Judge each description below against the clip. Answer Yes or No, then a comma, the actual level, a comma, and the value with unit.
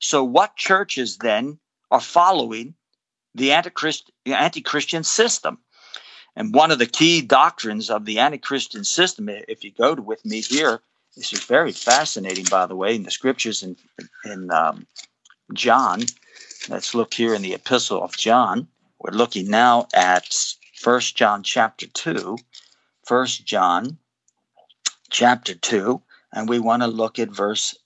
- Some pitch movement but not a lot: No, wide, 5.7 semitones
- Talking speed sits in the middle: Yes, average, 150 wpm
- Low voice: Yes, low, 120 Hz